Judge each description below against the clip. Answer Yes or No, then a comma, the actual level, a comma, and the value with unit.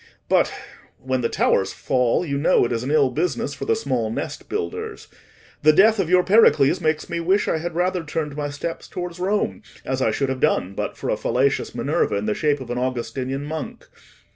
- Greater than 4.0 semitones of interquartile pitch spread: Yes, average, 5.1 semitones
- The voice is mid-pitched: Yes, medium, 145 Hz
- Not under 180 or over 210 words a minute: Yes, average, 200 wpm